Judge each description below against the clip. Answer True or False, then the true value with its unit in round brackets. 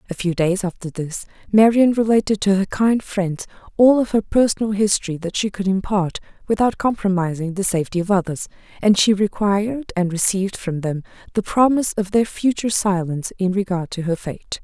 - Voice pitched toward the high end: True (200 Hz)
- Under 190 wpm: True (180 wpm)